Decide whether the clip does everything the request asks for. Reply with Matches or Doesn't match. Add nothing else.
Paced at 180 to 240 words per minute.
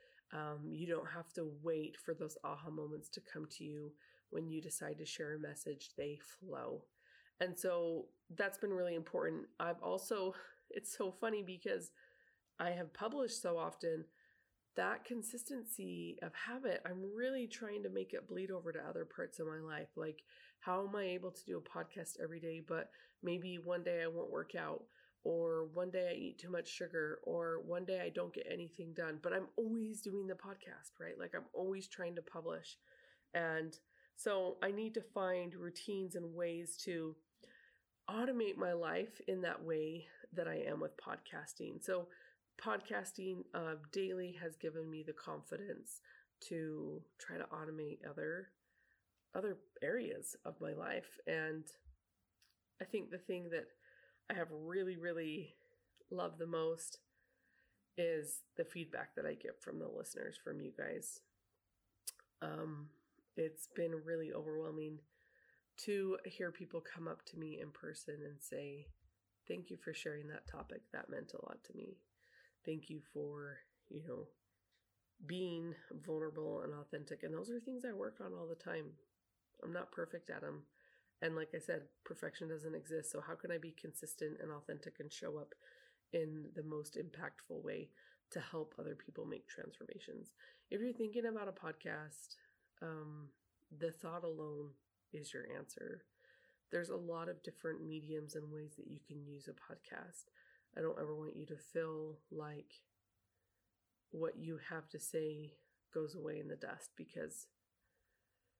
Doesn't match